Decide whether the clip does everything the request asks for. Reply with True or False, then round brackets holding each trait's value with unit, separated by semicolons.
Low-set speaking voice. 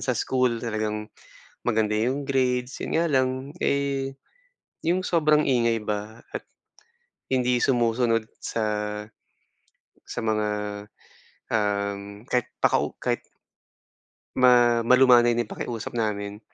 True (120 Hz)